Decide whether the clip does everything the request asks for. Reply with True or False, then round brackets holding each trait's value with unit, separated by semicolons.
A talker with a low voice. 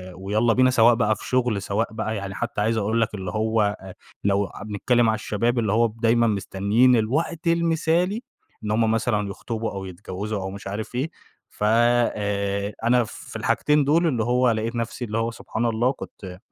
True (110 Hz)